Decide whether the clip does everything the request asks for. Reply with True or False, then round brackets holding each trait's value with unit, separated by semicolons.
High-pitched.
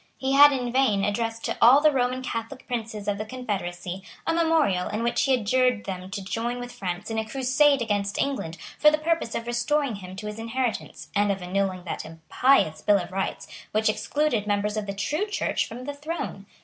True (225 Hz)